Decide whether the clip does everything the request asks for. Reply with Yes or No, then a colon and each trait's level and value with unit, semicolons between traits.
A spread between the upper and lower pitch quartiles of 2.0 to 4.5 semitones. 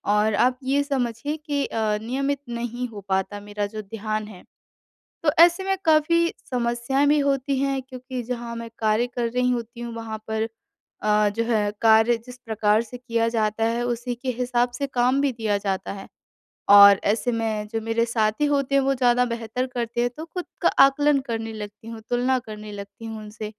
Yes: average, 3.0 semitones